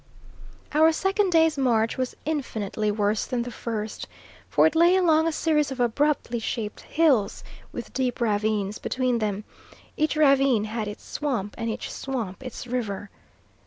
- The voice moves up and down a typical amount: No, wide, 5.8 semitones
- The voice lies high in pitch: Yes, high, 245 Hz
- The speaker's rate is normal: Yes, average, 155 wpm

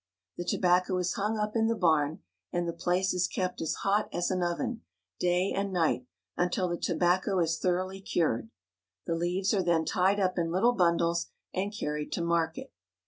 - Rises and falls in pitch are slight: Yes, narrow, 2.1 semitones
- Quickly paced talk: No, average, 185 wpm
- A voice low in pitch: No, medium, 180 Hz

